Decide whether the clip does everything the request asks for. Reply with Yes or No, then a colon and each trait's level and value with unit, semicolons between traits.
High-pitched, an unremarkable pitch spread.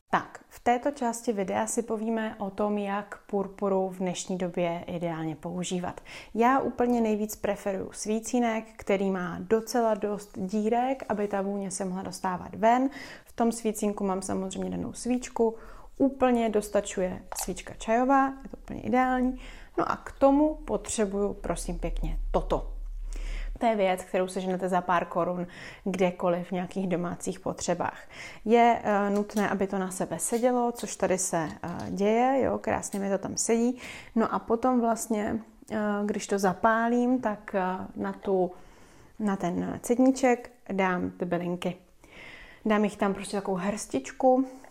Yes: high, 205 Hz; average, 3.8 semitones